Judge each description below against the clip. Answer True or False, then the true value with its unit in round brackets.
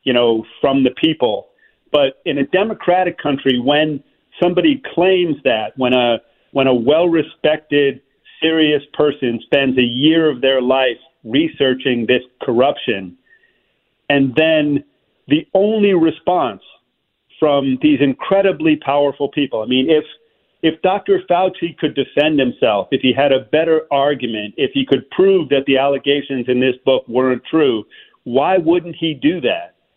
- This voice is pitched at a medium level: True (145 Hz)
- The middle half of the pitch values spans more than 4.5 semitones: False (4.1 semitones)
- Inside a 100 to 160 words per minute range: True (145 wpm)